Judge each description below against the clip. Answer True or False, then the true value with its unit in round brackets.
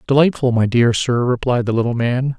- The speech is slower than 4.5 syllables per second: False (5.3 syllables/s)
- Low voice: True (125 Hz)